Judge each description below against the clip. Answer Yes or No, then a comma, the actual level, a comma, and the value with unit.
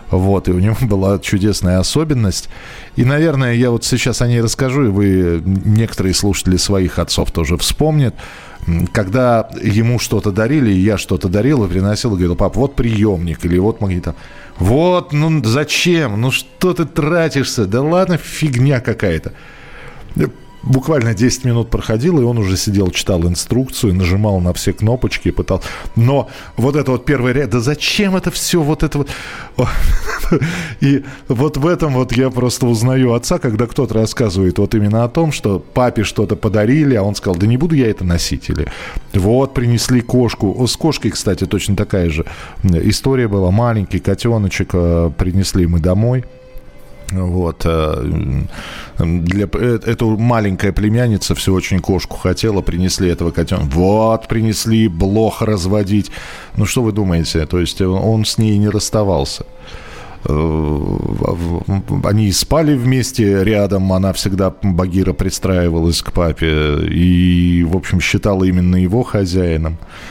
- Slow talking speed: No, average, 145 wpm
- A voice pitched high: No, low, 105 Hz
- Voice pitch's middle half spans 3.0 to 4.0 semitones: No, average, 5.3 semitones